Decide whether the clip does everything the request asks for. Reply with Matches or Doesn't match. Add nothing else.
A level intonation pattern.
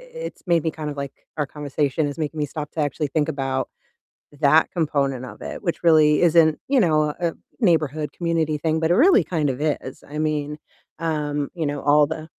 Matches